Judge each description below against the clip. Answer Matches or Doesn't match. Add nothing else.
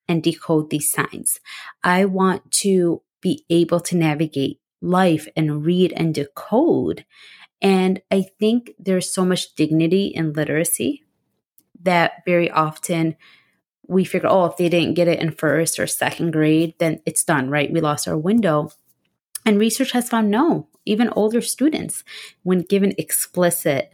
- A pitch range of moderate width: Matches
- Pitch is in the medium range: Matches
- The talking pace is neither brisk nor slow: Matches